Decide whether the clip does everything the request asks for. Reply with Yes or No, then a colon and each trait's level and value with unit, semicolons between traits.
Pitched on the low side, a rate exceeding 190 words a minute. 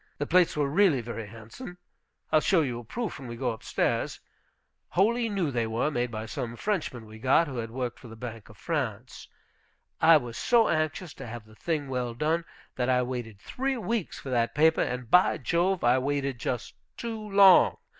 Yes: low, 130 Hz; average, 200 wpm